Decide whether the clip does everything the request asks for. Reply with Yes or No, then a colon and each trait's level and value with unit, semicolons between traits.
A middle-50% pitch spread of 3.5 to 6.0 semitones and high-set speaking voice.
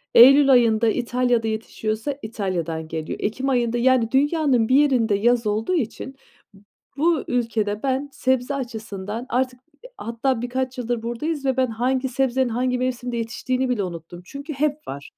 No: average, 2.9 semitones; high, 245 Hz